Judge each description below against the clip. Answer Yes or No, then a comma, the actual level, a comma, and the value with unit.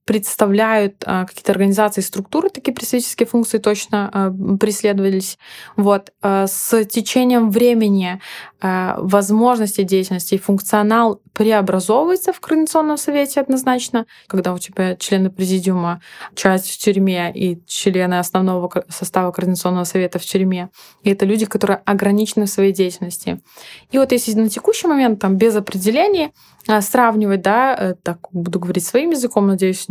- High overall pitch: Yes, high, 200 Hz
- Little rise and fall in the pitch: No, average, 3.5 semitones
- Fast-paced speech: No, average, 125 wpm